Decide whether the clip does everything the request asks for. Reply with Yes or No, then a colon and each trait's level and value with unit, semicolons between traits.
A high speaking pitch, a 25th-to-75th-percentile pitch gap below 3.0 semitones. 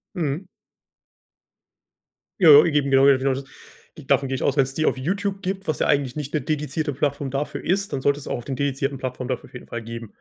No: medium, 140 Hz; narrow, 2.6 semitones